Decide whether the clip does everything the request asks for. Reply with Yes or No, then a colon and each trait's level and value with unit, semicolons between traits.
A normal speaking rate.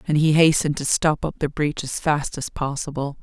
No: fast, 225 wpm